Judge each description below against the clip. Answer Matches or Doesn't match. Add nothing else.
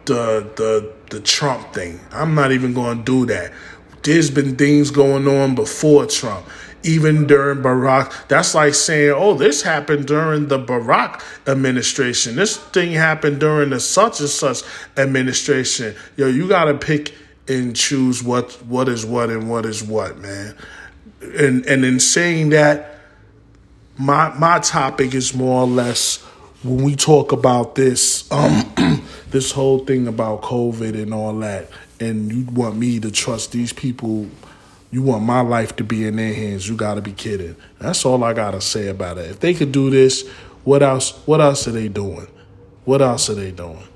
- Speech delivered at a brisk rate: Doesn't match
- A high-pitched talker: Doesn't match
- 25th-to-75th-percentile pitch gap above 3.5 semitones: Matches